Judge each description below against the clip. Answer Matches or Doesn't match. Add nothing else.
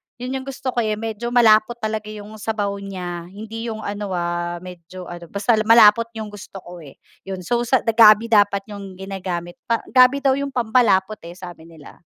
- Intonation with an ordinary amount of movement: Matches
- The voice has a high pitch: Matches